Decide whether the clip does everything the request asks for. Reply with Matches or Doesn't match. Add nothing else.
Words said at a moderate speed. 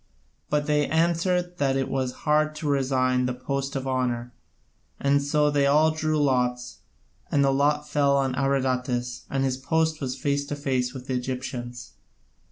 Matches